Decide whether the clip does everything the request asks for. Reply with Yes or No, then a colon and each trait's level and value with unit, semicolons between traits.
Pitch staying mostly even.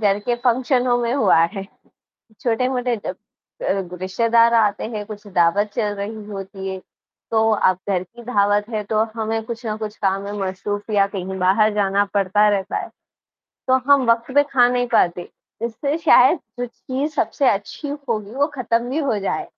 No: average, 3.2 semitones